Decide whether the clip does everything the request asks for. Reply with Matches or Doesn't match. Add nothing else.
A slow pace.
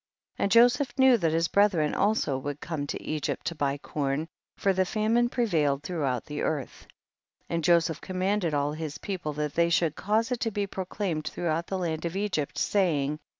Doesn't match